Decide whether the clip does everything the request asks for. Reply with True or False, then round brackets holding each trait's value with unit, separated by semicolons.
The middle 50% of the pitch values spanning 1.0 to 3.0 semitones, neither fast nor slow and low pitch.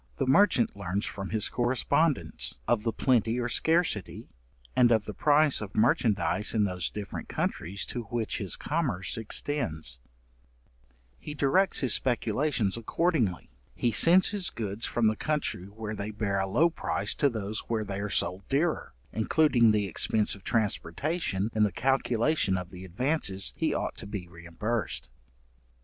False (5.4 semitones; 155 wpm; 110 Hz)